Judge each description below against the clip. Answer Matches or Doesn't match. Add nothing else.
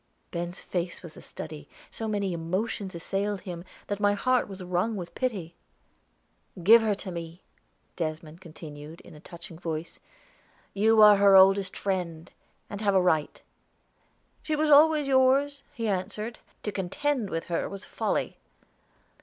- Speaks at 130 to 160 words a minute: Matches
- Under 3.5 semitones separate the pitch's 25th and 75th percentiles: Doesn't match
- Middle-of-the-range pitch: Doesn't match